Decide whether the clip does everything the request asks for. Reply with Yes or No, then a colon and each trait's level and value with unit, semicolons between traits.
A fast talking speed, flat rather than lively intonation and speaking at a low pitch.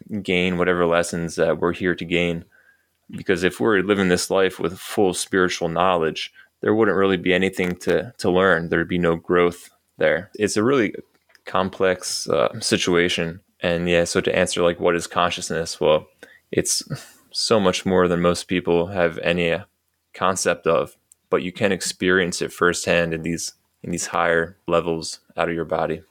No: average, 170 wpm; narrow, 1.3 semitones; very low, 85 Hz